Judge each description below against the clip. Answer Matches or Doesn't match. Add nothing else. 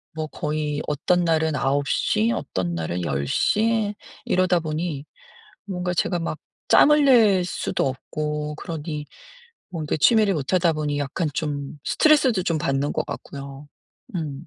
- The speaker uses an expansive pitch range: Doesn't match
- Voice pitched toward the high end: Doesn't match